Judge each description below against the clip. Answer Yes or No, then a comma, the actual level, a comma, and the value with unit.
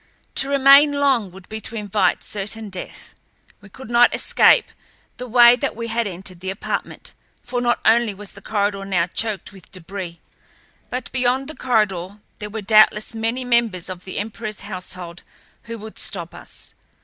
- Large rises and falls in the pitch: No, average, 3.8 semitones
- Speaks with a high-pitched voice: Yes, high, 215 Hz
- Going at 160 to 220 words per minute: Yes, average, 170 wpm